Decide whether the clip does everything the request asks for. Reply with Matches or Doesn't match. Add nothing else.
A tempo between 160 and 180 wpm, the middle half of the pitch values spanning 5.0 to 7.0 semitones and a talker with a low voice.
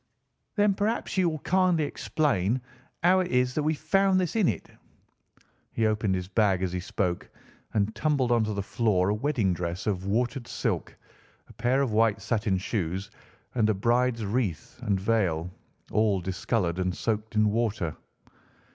Matches